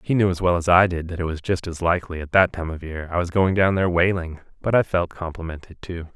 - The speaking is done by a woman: No, male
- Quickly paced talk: Yes, fast, 285 wpm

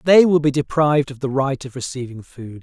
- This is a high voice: No, medium, 140 Hz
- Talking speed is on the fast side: Yes, fast, 230 wpm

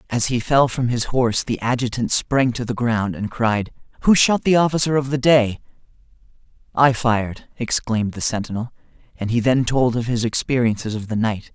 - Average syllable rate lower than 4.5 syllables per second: No, 5.2 syllables/s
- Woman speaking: No, male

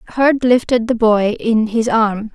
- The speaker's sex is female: Yes, female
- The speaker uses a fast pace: No, average, 180 wpm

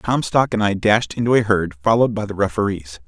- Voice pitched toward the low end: Yes, low, 105 Hz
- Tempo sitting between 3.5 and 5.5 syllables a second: No, 5.7 syllables/s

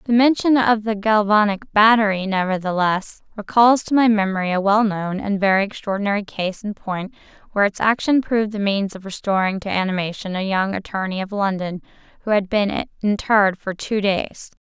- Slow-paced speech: No, average, 170 wpm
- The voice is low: No, high, 205 Hz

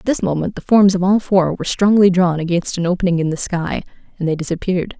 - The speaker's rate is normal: No, fast, 240 wpm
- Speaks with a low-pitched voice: No, medium, 180 Hz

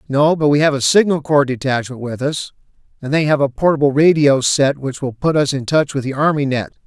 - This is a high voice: No, medium, 140 Hz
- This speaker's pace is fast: Yes, fast, 235 wpm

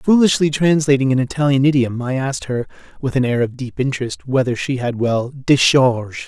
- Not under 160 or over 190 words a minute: Yes, average, 180 wpm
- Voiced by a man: Yes, male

